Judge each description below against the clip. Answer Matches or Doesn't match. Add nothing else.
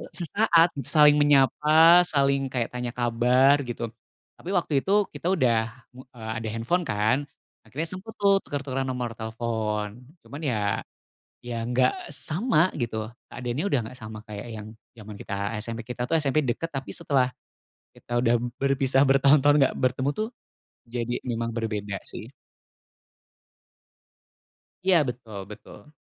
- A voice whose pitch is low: Matches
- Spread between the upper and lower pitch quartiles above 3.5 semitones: Matches